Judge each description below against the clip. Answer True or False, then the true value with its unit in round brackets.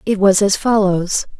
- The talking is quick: False (170 wpm)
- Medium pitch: False (200 Hz)